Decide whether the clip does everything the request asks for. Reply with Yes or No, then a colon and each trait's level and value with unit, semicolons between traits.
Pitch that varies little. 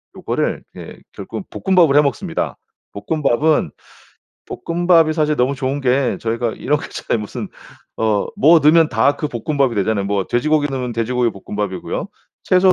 No: average, 5.2 semitones